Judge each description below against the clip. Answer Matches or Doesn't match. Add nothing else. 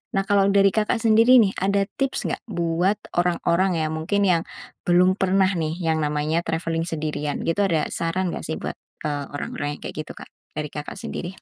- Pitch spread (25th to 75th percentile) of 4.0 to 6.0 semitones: Doesn't match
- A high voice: Doesn't match